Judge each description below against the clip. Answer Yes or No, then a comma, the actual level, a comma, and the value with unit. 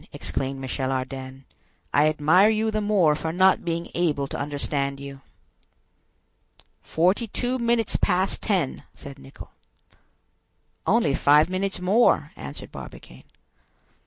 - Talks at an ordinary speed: No, slow, 120 wpm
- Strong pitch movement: Yes, wide, 6.2 semitones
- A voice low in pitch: No, medium, 160 Hz